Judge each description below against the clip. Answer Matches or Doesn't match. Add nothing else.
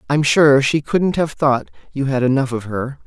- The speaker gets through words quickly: Matches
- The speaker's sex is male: Matches